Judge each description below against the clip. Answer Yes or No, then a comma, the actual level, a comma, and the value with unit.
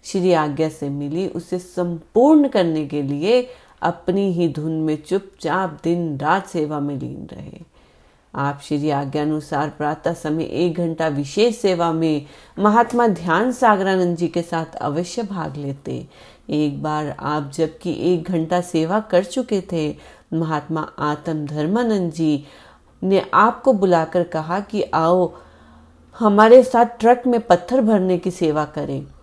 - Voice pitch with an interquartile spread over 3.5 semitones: Yes, average, 4.1 semitones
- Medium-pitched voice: Yes, medium, 170 Hz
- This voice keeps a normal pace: Yes, average, 140 wpm